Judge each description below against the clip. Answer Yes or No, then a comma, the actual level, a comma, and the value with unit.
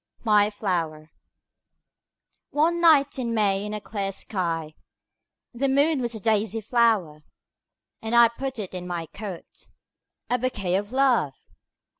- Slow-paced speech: Yes, slow, 115 wpm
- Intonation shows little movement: No, wide, 5.5 semitones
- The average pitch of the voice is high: Yes, high, 210 Hz